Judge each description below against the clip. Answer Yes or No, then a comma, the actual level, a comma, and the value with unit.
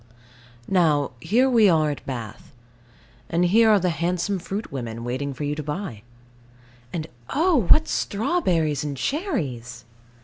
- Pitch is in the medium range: Yes, medium, 165 Hz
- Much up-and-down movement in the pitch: Yes, wide, 7.0 semitones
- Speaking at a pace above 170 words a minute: No, average, 140 wpm